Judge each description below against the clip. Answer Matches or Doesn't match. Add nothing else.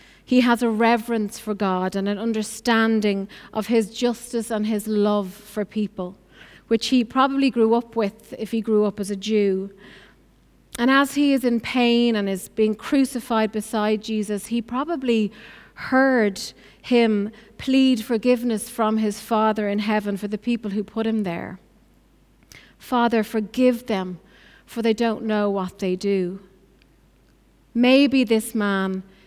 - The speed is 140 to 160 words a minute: Matches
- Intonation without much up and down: Matches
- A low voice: Doesn't match